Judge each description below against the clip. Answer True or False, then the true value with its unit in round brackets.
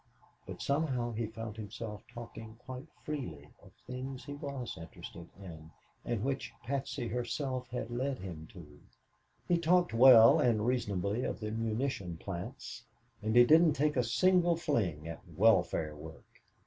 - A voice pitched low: True (115 Hz)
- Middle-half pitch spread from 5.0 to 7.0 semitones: True (5.3 semitones)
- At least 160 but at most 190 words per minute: False (150 wpm)